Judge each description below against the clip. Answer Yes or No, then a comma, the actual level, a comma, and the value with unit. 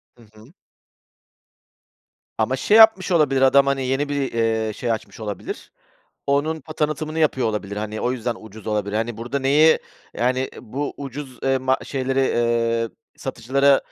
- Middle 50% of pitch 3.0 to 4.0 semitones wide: Yes, average, 3.6 semitones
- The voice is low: Yes, low, 130 Hz